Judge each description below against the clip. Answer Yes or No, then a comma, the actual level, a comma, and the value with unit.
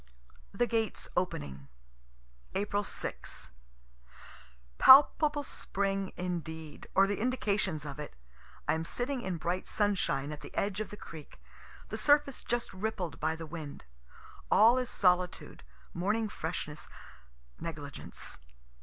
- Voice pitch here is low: No, high, 190 Hz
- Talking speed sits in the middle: No, slow, 120 wpm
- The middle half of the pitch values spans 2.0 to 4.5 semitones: No, wide, 5.4 semitones